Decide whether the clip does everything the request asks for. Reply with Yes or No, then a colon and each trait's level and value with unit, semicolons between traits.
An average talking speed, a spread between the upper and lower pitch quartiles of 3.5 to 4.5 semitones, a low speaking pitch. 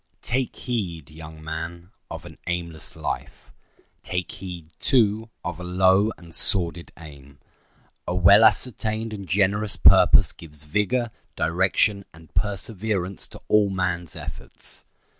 No: slow, 125 wpm; average, 3.8 semitones; very low, 90 Hz